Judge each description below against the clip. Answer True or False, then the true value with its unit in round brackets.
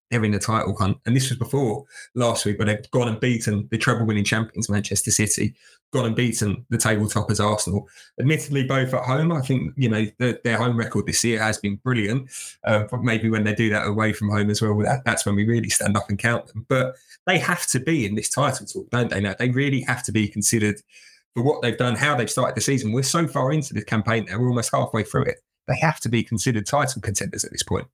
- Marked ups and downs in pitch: False (3.2 semitones)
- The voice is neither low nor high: False (115 Hz)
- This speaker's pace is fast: True (250 wpm)